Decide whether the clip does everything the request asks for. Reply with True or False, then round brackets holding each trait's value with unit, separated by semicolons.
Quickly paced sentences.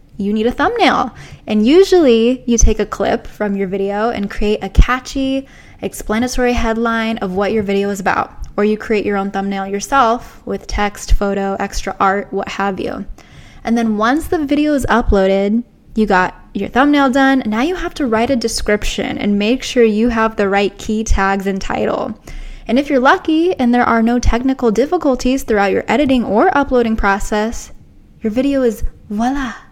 False (180 wpm)